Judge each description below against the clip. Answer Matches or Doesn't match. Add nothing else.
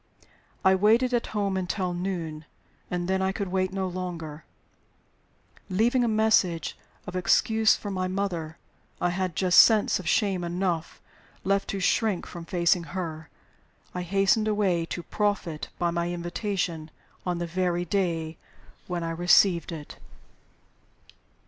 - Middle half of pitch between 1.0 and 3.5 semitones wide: Matches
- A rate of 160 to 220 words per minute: Doesn't match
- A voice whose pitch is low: Doesn't match